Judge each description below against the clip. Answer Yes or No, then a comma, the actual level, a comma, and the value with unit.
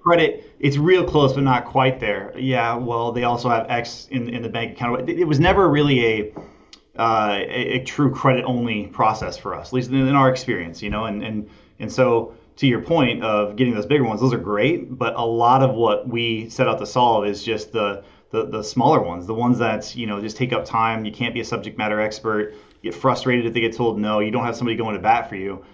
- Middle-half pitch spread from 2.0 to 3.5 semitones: Yes, average, 3.1 semitones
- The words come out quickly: Yes, fast, 240 wpm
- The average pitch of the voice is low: Yes, low, 115 Hz